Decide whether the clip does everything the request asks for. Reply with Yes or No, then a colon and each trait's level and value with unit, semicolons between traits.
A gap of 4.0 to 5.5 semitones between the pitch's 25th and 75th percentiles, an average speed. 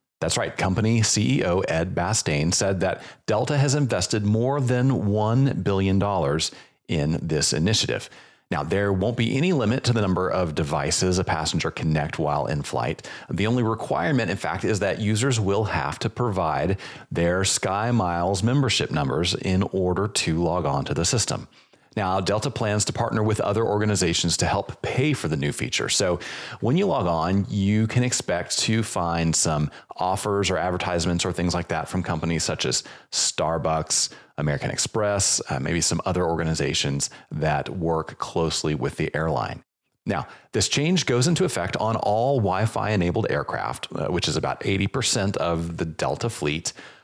Yes: average, 4.8 semitones; average, 170 wpm